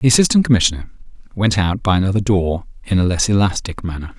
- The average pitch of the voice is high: No, low, 100 Hz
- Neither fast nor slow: Yes, average, 185 wpm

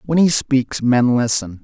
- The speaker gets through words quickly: No, average, 185 wpm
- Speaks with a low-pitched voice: Yes, low, 130 Hz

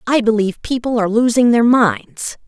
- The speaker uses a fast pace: No, average, 170 wpm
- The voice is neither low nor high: No, high, 225 Hz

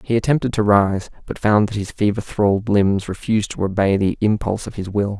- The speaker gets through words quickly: Yes, fast, 220 wpm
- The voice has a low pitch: Yes, low, 105 Hz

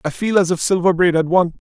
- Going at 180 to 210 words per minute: No, fast, 280 wpm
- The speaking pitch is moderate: Yes, medium, 175 Hz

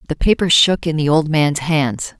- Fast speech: Yes, fast, 220 wpm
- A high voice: No, medium, 155 Hz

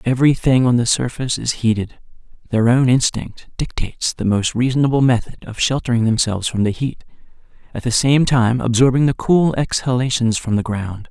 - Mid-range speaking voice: No, low, 120 Hz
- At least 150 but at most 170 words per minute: Yes, average, 165 wpm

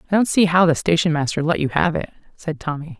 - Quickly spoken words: Yes, fast, 260 wpm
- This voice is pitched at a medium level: Yes, medium, 165 Hz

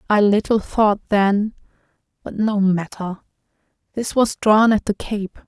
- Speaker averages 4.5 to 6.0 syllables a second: No, 4.0 syllables/s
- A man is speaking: No, female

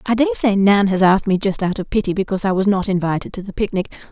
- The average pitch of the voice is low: No, high, 200 Hz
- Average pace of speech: No, fast, 275 wpm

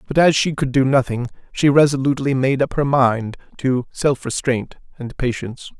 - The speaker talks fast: No, average, 175 wpm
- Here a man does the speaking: Yes, male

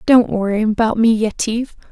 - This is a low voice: No, high, 220 Hz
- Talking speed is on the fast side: No, average, 155 wpm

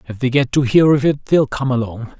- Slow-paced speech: No, fast, 275 wpm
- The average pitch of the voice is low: Yes, low, 130 Hz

